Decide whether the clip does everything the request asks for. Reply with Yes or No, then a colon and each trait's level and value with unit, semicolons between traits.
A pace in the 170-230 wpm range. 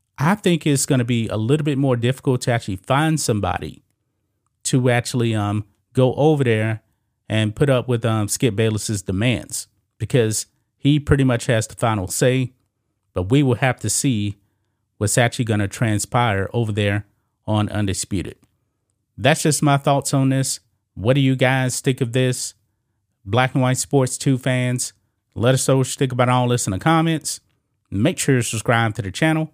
Yes: average, 180 wpm